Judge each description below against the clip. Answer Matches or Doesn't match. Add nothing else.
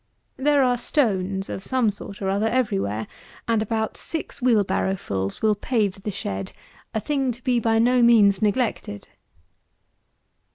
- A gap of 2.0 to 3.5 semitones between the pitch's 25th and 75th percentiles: Doesn't match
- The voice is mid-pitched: Doesn't match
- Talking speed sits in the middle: Matches